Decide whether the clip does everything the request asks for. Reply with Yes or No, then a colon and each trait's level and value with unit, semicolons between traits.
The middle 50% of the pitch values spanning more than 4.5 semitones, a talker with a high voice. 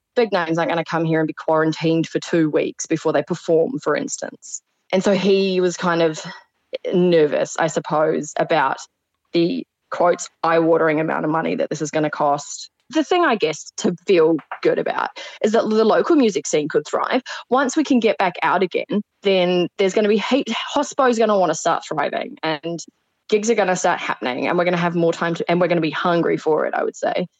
No: average, 4.9 semitones; medium, 175 Hz